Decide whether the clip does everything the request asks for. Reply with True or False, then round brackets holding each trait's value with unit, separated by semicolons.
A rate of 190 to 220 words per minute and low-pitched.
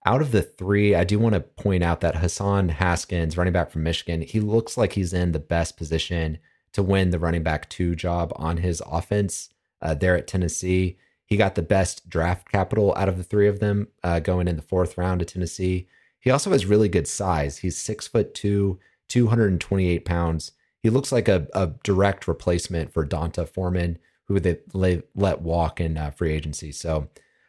True (200 wpm; 90 Hz)